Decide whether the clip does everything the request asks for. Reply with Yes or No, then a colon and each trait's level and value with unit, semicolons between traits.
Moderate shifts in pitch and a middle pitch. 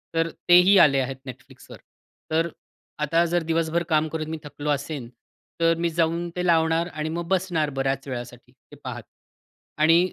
No: narrow, 2.3 semitones; medium, 160 Hz